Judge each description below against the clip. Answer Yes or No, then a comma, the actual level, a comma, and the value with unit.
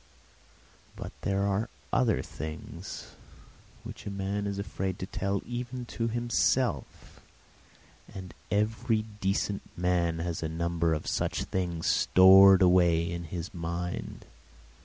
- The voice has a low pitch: Yes, very low, 95 Hz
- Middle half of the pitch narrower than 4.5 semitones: Yes, average, 3.2 semitones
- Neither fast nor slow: No, slow, 120 wpm